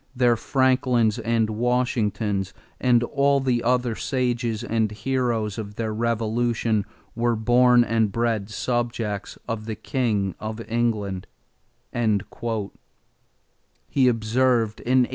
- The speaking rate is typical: No, slow, 110 wpm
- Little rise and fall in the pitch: Yes, narrow, 2.2 semitones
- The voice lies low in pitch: Yes, low, 115 Hz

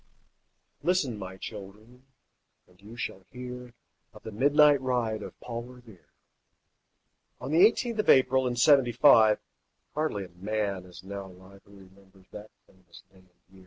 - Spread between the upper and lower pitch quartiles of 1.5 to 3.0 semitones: No, average, 4.9 semitones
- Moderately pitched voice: No, low, 110 Hz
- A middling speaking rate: Yes, average, 155 wpm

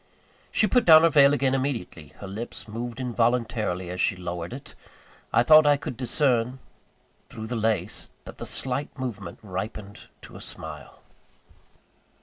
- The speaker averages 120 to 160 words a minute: Yes, average, 150 wpm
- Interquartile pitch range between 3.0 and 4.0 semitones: No, average, 5.2 semitones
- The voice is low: Yes, low, 115 Hz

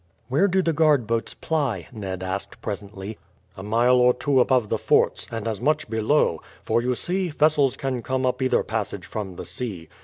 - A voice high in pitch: No, low, 125 Hz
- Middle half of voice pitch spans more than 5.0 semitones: Yes, wide, 5.5 semitones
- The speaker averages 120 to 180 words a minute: No, average, 190 wpm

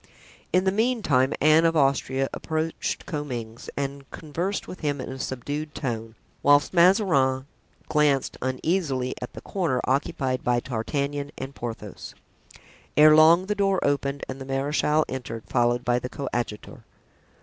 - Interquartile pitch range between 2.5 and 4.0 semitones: Yes, average, 3.5 semitones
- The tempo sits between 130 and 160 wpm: Yes, average, 140 wpm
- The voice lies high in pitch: No, medium, 140 Hz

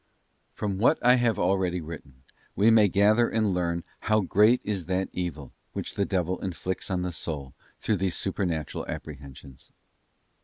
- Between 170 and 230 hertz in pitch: No, very low, 95 Hz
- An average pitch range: Yes, average, 3.7 semitones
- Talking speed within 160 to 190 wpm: No, average, 150 wpm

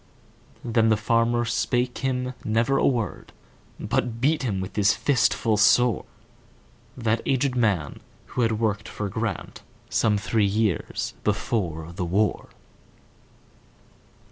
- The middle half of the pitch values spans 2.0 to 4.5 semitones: Yes, average, 2.7 semitones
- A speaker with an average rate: No, slow, 110 wpm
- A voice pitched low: Yes, low, 115 Hz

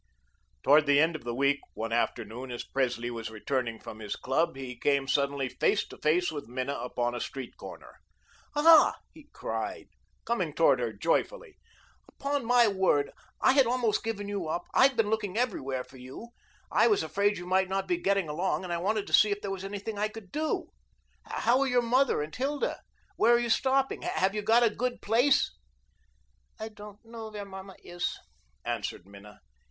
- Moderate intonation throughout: No, wide, 8.8 semitones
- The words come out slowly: No, average, 190 wpm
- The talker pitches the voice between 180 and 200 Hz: Yes, high, 190 Hz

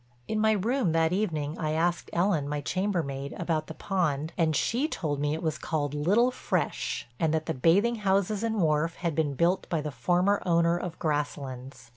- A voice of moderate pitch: Yes, medium, 165 Hz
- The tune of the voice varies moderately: Yes, average, 4.3 semitones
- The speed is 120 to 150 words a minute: No, average, 190 wpm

